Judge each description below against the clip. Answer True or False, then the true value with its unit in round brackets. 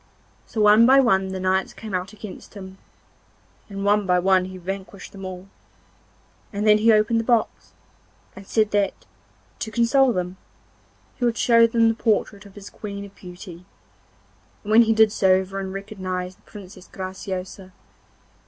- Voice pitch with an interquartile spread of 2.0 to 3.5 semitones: True (2.5 semitones)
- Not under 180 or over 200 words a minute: False (165 wpm)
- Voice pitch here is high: True (200 Hz)